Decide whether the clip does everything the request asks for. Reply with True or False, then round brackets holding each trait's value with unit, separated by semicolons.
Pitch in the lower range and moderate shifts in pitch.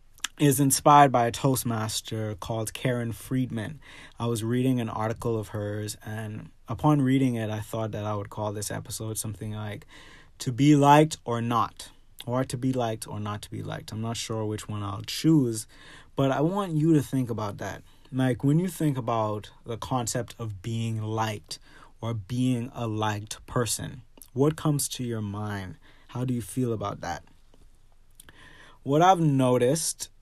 True (115 Hz; 4.1 semitones)